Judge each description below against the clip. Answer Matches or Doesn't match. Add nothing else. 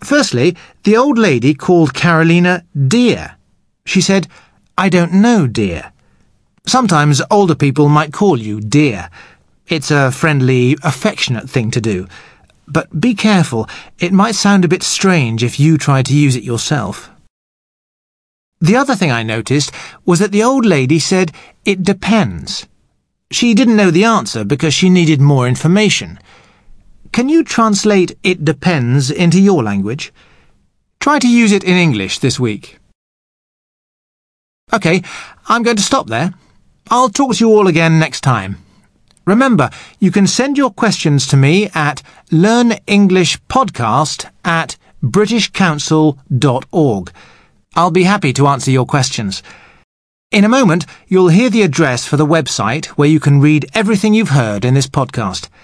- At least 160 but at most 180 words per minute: Doesn't match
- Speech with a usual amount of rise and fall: Doesn't match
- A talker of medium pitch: Matches